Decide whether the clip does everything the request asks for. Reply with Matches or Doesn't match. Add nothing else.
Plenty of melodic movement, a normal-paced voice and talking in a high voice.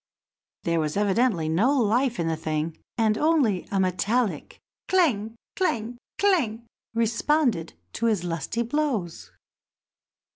Doesn't match